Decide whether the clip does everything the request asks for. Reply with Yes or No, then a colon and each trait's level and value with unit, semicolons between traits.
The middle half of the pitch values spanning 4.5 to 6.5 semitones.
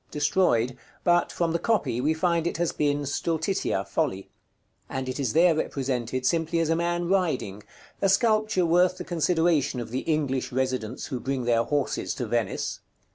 Yes: average, 5.2 semitones